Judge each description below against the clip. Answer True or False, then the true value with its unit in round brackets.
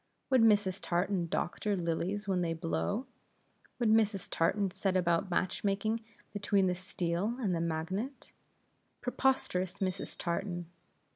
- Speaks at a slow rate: True (125 wpm)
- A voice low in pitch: False (190 Hz)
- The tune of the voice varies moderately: True (3.1 semitones)